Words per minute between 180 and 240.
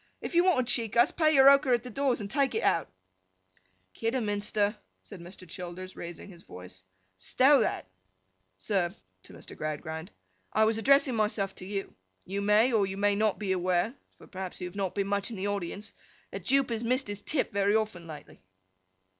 Yes: average, 190 wpm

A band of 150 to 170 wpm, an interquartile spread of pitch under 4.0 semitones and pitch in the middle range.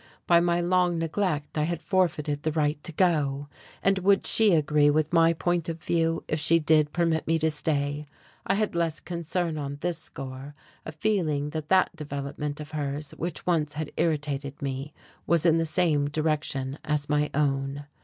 No: average, 180 wpm; narrow, 2.6 semitones; medium, 155 Hz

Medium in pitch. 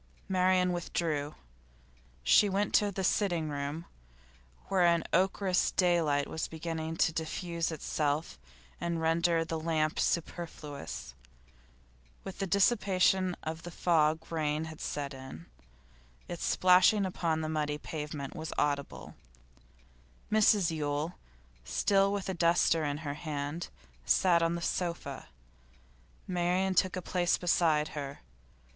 Yes: medium, 165 Hz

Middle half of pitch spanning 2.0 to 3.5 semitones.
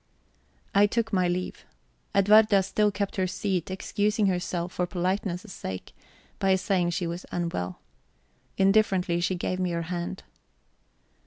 Yes: narrow, 2.4 semitones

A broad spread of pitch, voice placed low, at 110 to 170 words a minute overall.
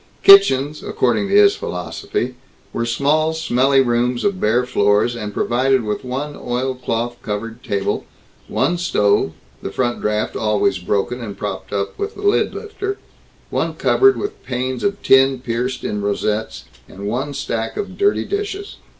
Yes: wide, 6.0 semitones; low, 125 Hz; average, 150 wpm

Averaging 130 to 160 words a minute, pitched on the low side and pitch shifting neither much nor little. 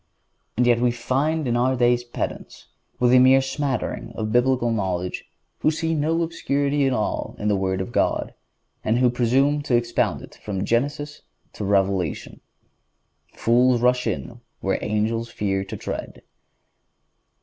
Yes: average, 150 wpm; low, 120 Hz; average, 3.8 semitones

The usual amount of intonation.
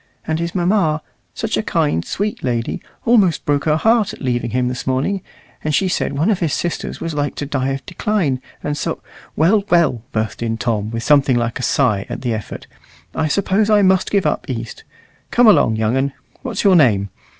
No: wide, 7.5 semitones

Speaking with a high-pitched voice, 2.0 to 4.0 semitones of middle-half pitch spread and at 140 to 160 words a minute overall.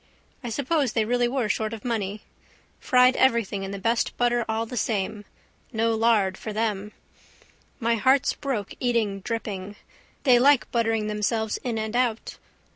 Yes: high, 225 Hz; narrow, 2.4 semitones; average, 155 wpm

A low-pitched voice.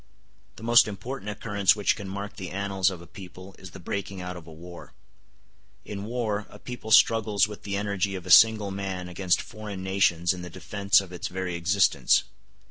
Yes: low, 100 Hz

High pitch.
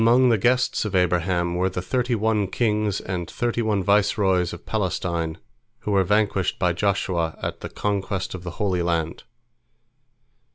No: very low, 95 Hz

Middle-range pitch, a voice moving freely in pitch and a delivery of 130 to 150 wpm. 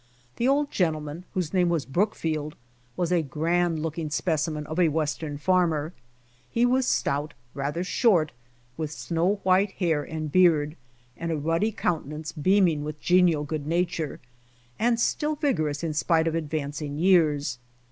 No: medium, 160 Hz; average, 3.1 semitones; average, 145 wpm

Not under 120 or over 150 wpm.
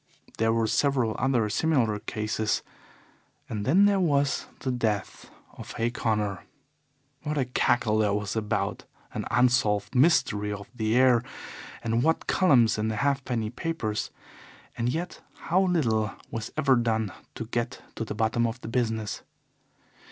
Yes: average, 145 wpm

